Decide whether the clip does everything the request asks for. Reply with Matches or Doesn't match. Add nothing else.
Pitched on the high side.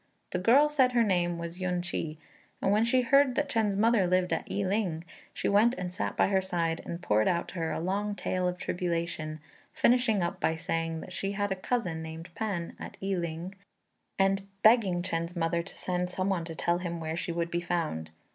Doesn't match